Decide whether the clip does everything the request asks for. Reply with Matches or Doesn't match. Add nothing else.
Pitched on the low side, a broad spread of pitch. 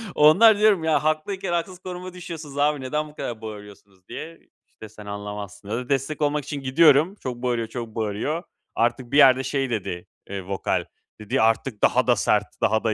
Matches